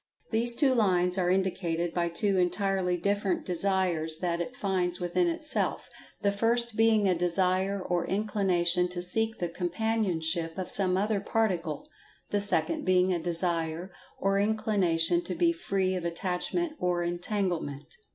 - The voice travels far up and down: No, average, 2.8 semitones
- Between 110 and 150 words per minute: Yes, average, 140 wpm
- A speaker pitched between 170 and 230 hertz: Yes, medium, 185 Hz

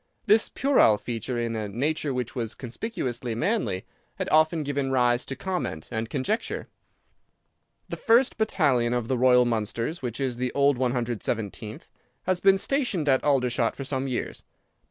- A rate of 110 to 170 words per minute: Yes, average, 155 wpm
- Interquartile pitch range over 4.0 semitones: Yes, average, 4.7 semitones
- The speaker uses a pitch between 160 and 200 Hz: No, low, 130 Hz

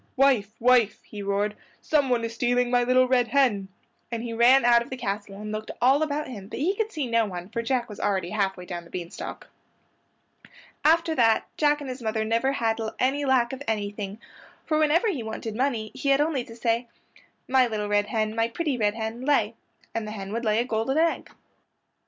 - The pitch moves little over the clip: No, average, 3.7 semitones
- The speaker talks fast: Yes, fast, 210 wpm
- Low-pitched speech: No, high, 235 Hz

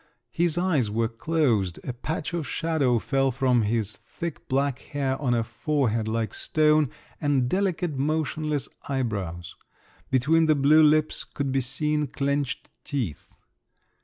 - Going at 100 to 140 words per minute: Yes, slow, 135 wpm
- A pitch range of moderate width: Yes, average, 4.3 semitones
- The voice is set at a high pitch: No, medium, 140 Hz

